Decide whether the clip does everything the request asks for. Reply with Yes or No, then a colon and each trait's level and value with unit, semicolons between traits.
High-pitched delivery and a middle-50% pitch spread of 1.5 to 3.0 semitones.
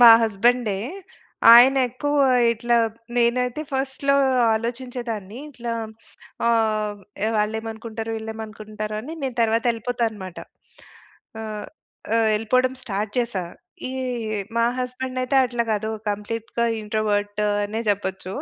Yes: high, 225 Hz; narrow, 2.5 semitones